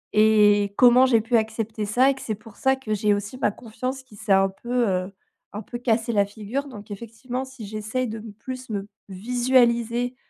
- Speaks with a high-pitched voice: Yes, high, 225 Hz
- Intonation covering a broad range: No, average, 3.2 semitones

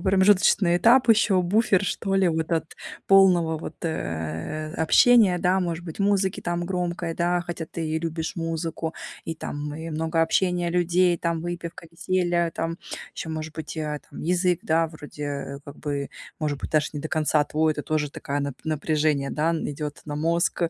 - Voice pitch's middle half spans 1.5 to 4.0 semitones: Yes, narrow, 2.4 semitones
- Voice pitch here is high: No, medium, 165 Hz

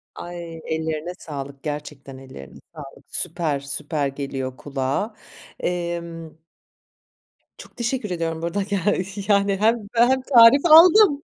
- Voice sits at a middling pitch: Yes, medium, 170 Hz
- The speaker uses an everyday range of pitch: No, wide, 6.5 semitones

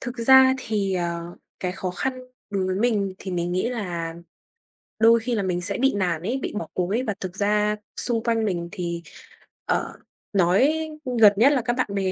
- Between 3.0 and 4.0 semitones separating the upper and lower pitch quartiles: No, average, 4.5 semitones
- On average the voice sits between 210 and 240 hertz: No, high, 200 Hz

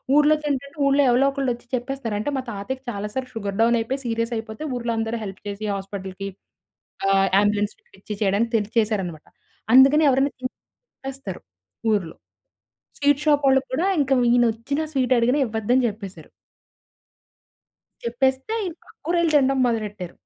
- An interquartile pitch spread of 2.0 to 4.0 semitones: No, average, 4.5 semitones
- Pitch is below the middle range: No, high, 235 Hz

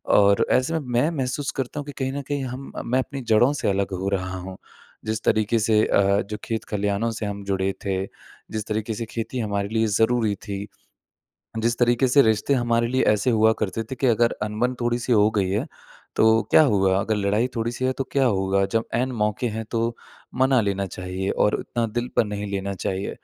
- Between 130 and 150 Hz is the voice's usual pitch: No, low, 110 Hz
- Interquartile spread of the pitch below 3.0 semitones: No, average, 3.4 semitones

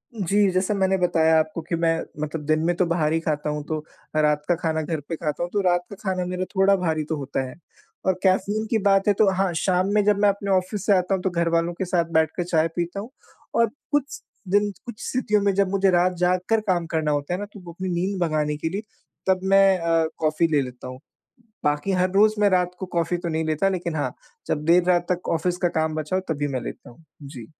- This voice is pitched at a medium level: Yes, medium, 175 Hz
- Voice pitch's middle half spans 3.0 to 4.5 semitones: Yes, average, 3.3 semitones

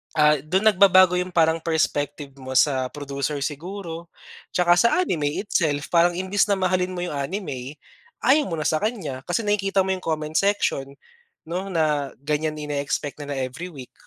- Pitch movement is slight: No, average, 4.3 semitones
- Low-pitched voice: No, medium, 160 Hz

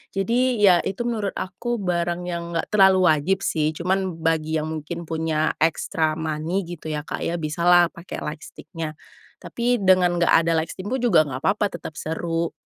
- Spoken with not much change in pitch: No, average, 3.1 semitones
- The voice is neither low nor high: Yes, medium, 170 Hz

